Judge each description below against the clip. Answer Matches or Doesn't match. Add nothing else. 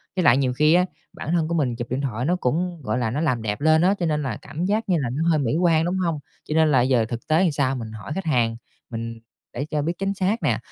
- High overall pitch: Doesn't match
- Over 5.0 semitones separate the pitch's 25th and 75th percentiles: Matches